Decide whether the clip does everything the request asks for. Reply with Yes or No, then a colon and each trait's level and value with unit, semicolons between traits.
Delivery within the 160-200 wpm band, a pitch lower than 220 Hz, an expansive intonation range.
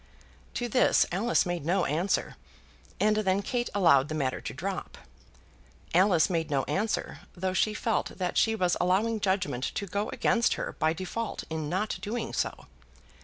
No: average, 165 wpm; high, 190 Hz; average, 4.3 semitones